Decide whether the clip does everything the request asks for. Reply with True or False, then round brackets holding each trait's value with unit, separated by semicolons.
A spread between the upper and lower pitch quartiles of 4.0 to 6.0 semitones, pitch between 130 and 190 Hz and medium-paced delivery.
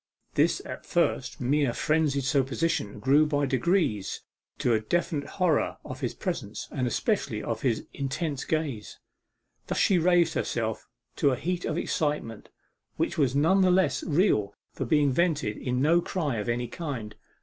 True (5.3 semitones; 140 Hz; 160 wpm)